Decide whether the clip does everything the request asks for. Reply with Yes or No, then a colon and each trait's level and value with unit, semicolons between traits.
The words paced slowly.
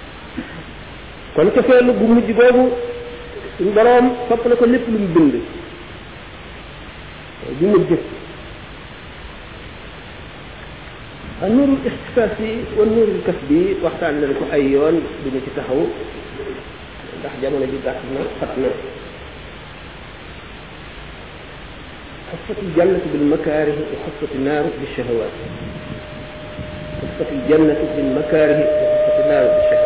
Yes: slow, 50 wpm